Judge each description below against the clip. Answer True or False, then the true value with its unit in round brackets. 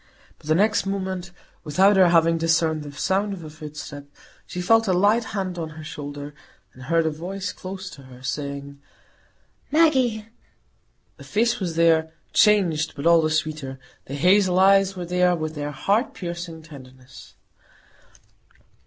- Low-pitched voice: False (165 Hz)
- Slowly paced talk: False (155 wpm)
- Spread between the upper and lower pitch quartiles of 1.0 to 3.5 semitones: False (4.2 semitones)